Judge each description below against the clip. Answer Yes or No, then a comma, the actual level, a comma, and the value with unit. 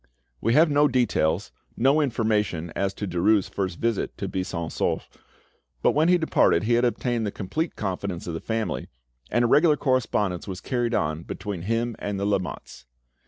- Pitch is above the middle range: No, low, 110 Hz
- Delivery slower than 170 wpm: No, average, 175 wpm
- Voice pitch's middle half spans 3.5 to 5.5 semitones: Yes, average, 4.6 semitones